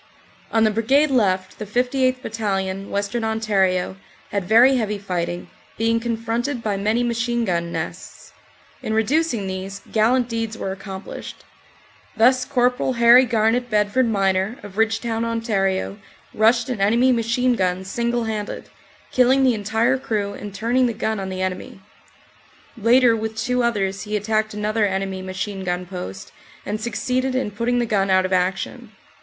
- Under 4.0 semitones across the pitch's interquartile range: Yes, average, 3.4 semitones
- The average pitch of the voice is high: Yes, high, 220 Hz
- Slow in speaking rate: No, average, 155 wpm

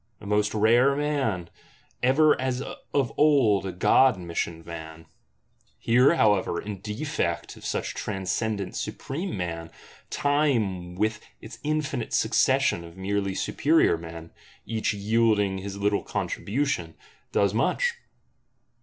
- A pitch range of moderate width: No, wide, 6.2 semitones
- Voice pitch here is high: No, low, 105 Hz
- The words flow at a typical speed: No, slow, 120 wpm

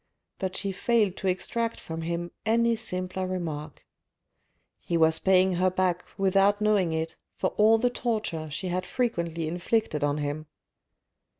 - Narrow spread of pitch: No, average, 4.4 semitones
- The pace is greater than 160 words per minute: No, average, 145 wpm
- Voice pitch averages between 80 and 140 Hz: No, medium, 185 Hz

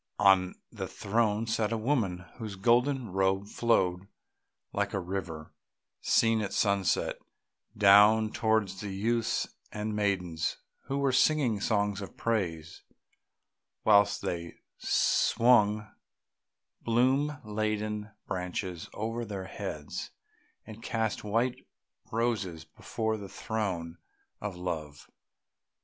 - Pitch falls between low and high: No, low, 105 Hz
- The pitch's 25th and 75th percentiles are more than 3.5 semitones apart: No, average, 3.0 semitones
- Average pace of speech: No, slow, 105 wpm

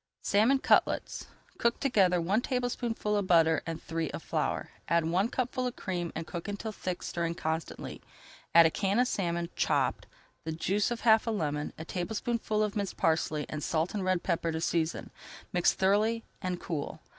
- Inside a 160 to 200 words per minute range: Yes, average, 180 wpm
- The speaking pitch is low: No, medium, 185 Hz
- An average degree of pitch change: Yes, average, 4.8 semitones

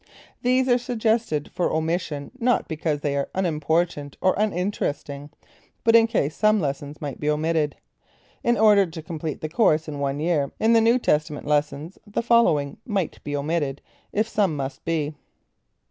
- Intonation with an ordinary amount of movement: No, wide, 6.4 semitones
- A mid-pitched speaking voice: Yes, medium, 160 Hz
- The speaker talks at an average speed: Yes, average, 160 wpm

